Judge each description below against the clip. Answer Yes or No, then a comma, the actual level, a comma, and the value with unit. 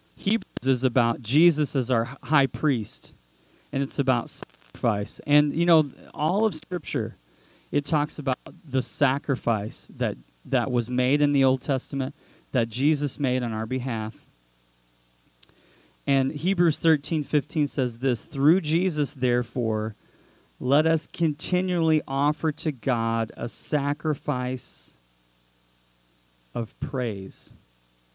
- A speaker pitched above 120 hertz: Yes, low, 135 Hz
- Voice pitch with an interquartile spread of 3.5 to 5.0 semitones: Yes, average, 4.6 semitones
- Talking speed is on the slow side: Yes, slow, 120 wpm